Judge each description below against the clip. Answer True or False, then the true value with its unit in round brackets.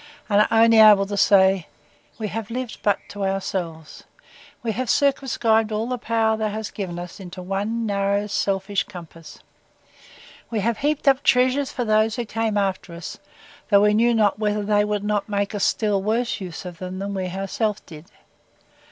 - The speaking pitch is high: True (210 Hz)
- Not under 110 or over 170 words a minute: False (180 wpm)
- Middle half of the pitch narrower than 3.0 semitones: True (2.5 semitones)